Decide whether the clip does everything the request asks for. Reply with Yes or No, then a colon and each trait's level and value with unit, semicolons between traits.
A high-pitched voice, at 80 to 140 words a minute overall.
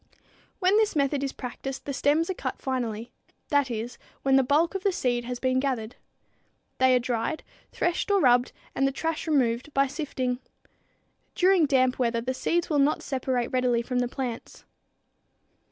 No: very high, 265 Hz; average, 170 wpm